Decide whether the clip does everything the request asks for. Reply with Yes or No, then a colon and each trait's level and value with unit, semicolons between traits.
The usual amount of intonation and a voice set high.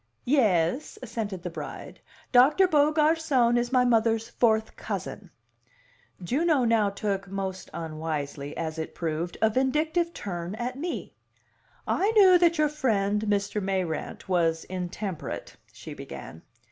No: wide, 7.2 semitones; high, 220 Hz